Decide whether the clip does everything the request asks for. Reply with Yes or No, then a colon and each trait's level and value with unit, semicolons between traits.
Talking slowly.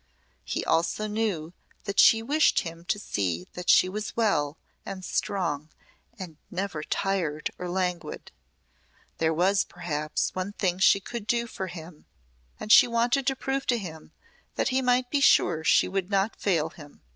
No: average, 165 wpm